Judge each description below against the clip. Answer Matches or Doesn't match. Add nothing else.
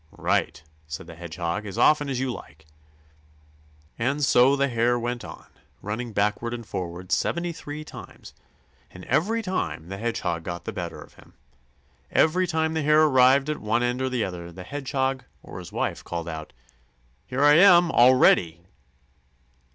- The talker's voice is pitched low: Matches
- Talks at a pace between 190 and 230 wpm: Doesn't match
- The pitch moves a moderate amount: Doesn't match